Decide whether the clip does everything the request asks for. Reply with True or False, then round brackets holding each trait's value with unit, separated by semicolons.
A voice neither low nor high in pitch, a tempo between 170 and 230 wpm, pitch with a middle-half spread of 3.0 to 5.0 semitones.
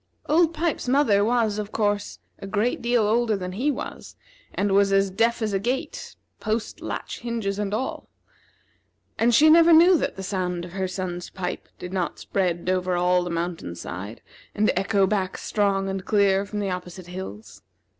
False (200 Hz; 175 wpm; 3.7 semitones)